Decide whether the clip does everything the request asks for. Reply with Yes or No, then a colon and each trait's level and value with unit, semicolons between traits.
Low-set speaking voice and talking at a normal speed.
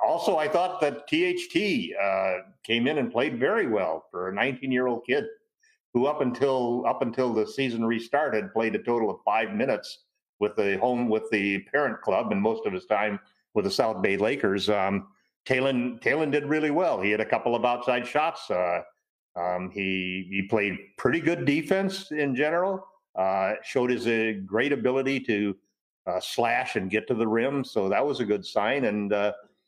Yes: low, 120 Hz; average, 185 wpm